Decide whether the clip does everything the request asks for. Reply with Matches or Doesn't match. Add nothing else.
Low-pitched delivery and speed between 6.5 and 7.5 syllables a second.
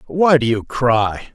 Doesn't match